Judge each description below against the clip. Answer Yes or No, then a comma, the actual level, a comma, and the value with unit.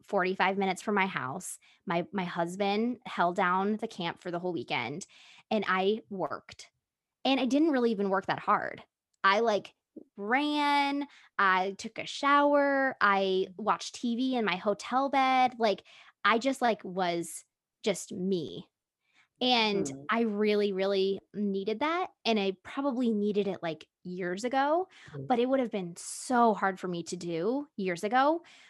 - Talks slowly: No, average, 155 wpm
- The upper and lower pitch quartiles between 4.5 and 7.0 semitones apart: Yes, average, 5.1 semitones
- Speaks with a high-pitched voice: Yes, high, 205 Hz